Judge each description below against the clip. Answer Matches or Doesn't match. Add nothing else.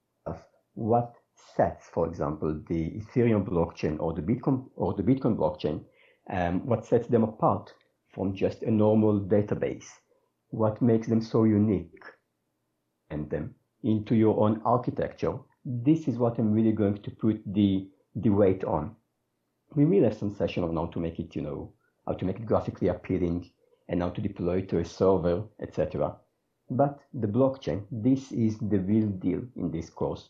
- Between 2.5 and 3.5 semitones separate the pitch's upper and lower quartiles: Doesn't match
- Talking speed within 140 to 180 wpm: Matches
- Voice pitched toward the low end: Matches